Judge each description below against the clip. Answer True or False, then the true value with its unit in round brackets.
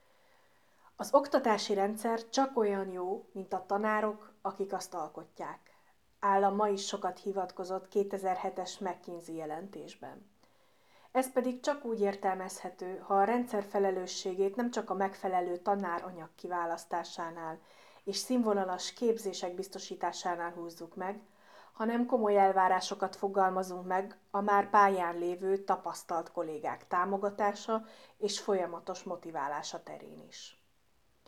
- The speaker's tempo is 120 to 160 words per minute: False (110 wpm)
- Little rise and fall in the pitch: True (2.1 semitones)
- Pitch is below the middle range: False (195 Hz)